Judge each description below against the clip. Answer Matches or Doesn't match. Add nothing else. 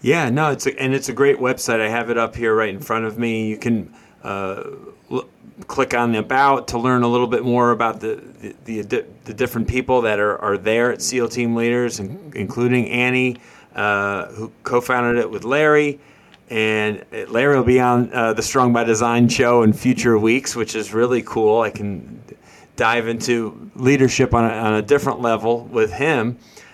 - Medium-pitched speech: Doesn't match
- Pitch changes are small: Matches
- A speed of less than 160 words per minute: Doesn't match